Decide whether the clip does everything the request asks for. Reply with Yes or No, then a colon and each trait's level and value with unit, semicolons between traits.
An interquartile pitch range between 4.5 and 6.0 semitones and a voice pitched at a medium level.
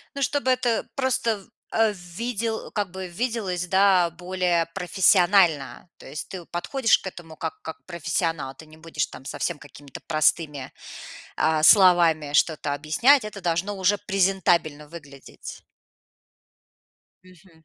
No: average, 4.1 semitones; medium, 175 Hz